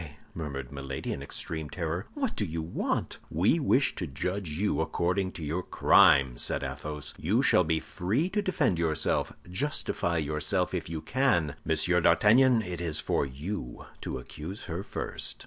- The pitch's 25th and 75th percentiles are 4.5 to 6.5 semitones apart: Yes, average, 4.9 semitones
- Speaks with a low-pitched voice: Yes, very low, 85 Hz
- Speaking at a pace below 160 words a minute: No, average, 165 wpm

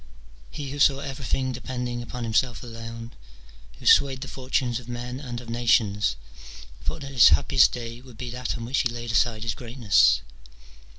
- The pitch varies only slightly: Yes, narrow, 2.0 semitones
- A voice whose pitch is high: No, low, 120 Hz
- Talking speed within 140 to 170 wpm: No, average, 180 wpm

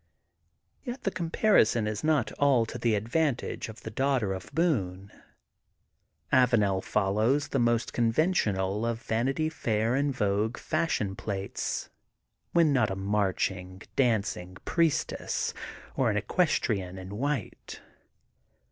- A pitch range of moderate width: No, wide, 6.0 semitones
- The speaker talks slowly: Yes, slow, 120 wpm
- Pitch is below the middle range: Yes, low, 115 Hz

